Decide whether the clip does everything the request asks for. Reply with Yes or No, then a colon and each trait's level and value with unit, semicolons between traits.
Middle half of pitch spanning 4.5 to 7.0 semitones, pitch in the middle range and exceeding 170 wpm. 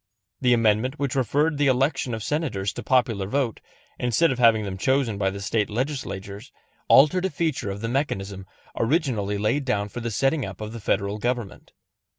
No: average, 4.9 semitones; low, 115 Hz; average, 180 wpm